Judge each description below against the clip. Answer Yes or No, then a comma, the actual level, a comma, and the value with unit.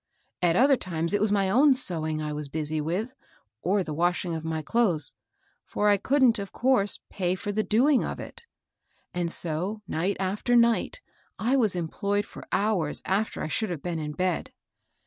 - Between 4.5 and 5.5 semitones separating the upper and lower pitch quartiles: Yes, average, 5.0 semitones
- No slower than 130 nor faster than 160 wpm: No, average, 190 wpm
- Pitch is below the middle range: No, high, 190 Hz